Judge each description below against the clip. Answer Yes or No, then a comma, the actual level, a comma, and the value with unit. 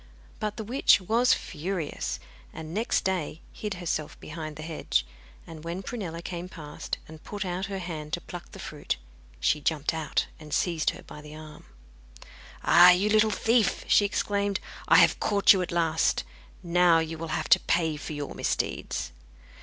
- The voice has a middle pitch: Yes, medium, 170 Hz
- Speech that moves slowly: No, average, 175 wpm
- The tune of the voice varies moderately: Yes, average, 3.9 semitones